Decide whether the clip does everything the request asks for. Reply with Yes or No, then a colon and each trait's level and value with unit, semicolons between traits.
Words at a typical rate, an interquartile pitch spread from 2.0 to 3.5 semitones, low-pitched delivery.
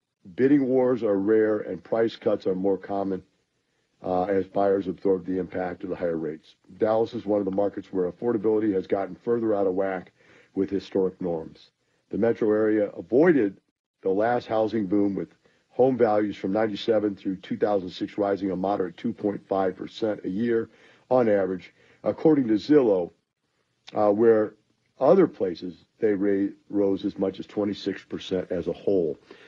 Yes: average, 155 wpm; narrow, 2.4 semitones; low, 100 Hz